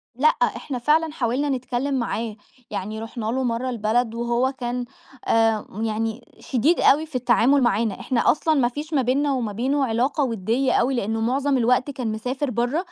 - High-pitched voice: Yes, high, 245 Hz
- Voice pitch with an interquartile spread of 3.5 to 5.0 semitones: No, average, 3.1 semitones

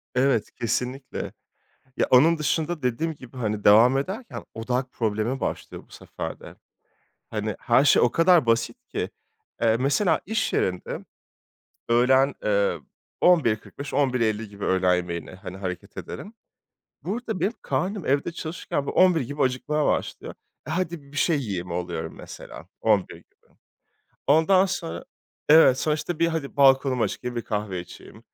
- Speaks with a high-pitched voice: No, low, 130 Hz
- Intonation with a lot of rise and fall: Yes, wide, 6.5 semitones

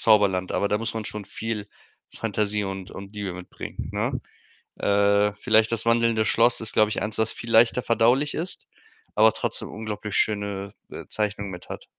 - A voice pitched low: Yes, low, 105 Hz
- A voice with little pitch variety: Yes, narrow, 1.8 semitones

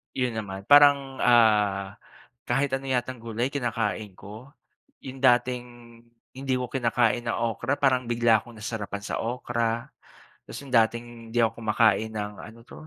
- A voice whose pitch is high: No, low, 120 Hz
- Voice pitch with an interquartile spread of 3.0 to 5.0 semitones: No, narrow, 2.6 semitones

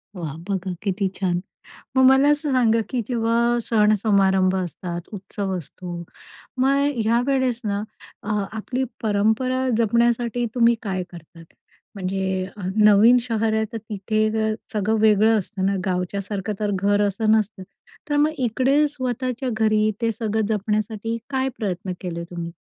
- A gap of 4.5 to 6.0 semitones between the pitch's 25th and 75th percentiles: No, average, 3.5 semitones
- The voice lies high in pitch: Yes, high, 215 Hz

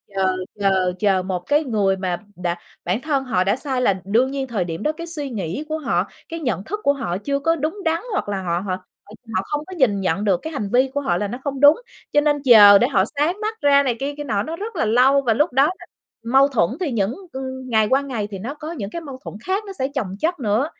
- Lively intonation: Yes, wide, 6.7 semitones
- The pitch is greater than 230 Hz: Yes, very high, 255 Hz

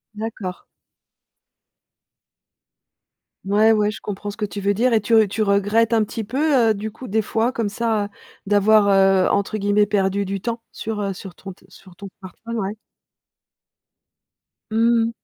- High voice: Yes, high, 210 Hz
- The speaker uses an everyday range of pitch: No, narrow, 2.0 semitones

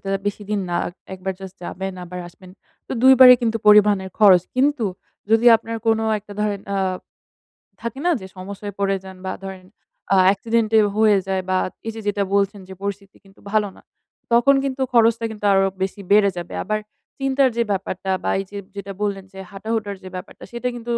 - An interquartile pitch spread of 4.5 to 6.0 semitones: No, average, 2.7 semitones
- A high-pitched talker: Yes, high, 205 Hz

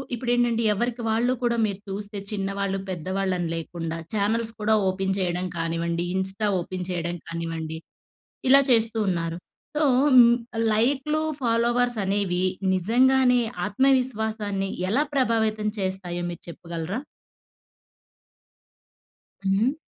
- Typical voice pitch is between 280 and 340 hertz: No, high, 200 Hz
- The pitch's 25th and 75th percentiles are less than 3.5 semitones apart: No, average, 4.7 semitones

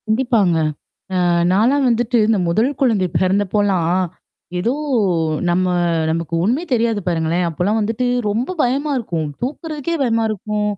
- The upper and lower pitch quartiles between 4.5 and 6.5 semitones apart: Yes, average, 5.0 semitones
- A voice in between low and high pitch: No, high, 215 Hz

